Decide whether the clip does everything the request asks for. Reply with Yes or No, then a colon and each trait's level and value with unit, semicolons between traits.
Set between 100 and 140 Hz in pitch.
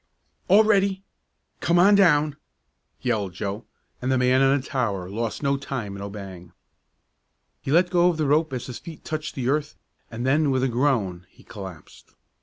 Yes: low, 135 Hz